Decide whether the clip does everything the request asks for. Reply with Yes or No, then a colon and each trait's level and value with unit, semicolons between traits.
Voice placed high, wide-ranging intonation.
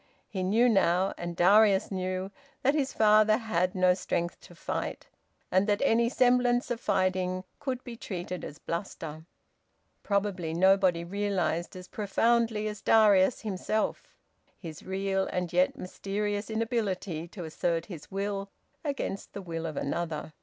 No: high, 195 Hz; average, 3.2 semitones